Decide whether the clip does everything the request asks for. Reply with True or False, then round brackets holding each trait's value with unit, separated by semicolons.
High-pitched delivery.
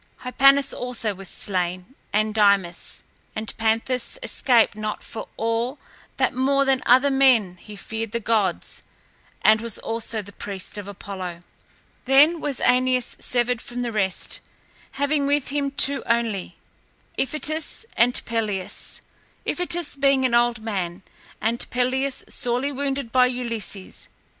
True (235 Hz)